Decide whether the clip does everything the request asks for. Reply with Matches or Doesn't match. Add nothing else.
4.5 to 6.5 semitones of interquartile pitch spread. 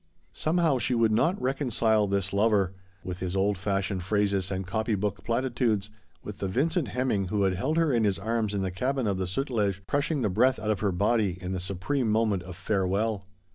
Doesn't match